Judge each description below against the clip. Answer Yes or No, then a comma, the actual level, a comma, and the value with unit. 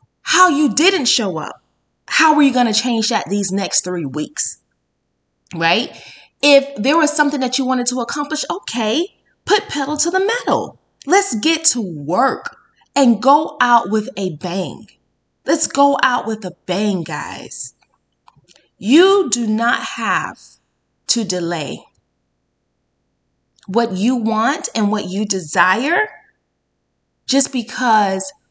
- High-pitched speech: Yes, high, 245 Hz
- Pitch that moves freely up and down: Yes, wide, 6.8 semitones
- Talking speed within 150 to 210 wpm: No, slow, 135 wpm